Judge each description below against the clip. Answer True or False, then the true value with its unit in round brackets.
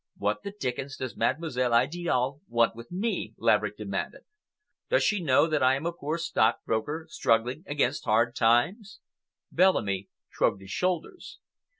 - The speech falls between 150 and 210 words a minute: False (140 wpm)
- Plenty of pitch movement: True (6.2 semitones)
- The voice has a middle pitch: False (130 Hz)